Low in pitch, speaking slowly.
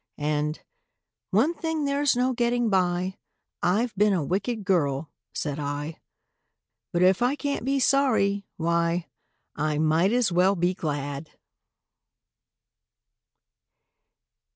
No: medium, 185 Hz; slow, 110 wpm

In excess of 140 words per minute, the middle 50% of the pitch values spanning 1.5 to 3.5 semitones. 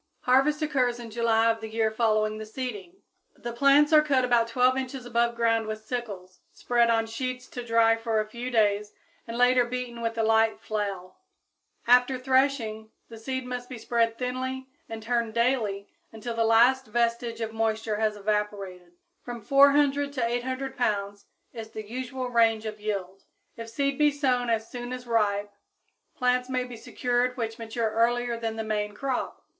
Yes: average, 175 wpm; narrow, 2.4 semitones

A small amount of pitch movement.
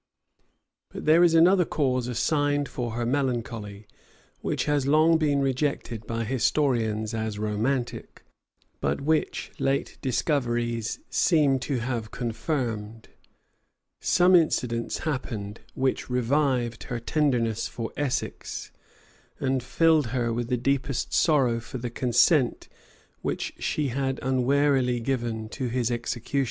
No: average, 3.5 semitones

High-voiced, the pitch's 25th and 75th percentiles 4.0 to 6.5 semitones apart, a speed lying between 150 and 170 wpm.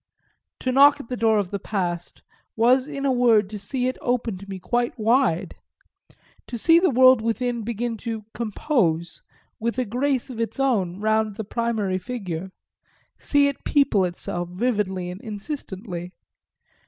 Yes: high, 225 Hz; average, 4.5 semitones; average, 160 wpm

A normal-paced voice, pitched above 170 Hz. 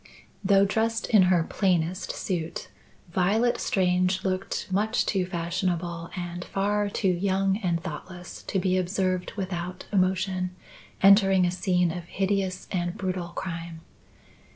No: slow, 130 wpm; medium, 185 Hz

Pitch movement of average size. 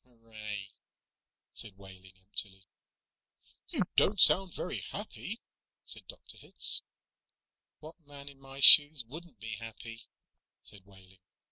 No: wide, 6.7 semitones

